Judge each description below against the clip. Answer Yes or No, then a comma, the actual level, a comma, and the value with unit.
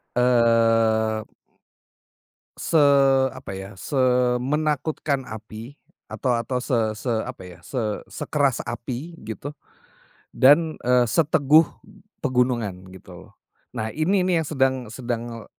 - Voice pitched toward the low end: Yes, low, 125 Hz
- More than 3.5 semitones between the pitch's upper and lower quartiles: Yes, average, 3.9 semitones